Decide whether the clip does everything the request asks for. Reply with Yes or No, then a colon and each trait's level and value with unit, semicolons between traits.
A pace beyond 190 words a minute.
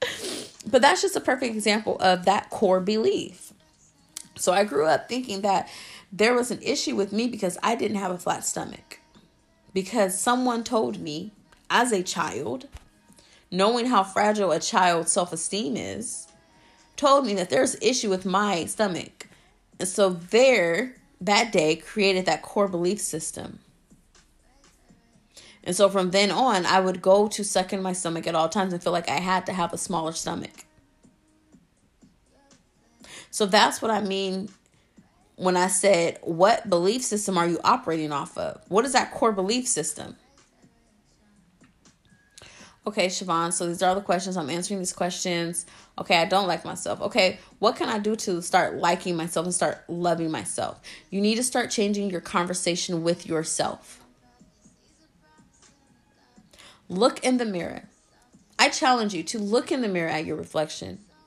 No: average, 160 wpm